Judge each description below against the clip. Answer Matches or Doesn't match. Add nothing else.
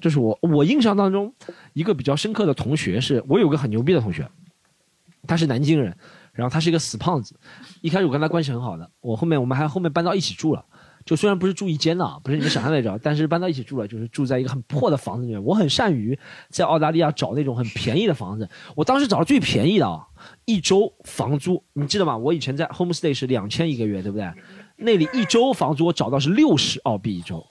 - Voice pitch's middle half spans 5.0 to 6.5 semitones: Matches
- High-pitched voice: Doesn't match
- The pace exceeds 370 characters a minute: Matches